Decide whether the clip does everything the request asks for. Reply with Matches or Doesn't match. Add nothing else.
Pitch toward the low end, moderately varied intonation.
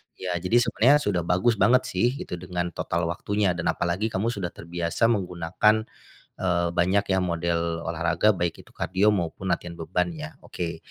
Matches